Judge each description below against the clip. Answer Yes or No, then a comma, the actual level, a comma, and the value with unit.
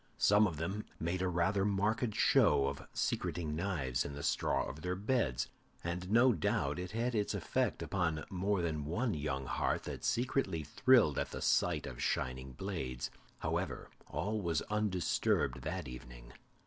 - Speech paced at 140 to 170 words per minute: Yes, average, 165 wpm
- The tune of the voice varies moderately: No, wide, 6.3 semitones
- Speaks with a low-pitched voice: Yes, very low, 90 Hz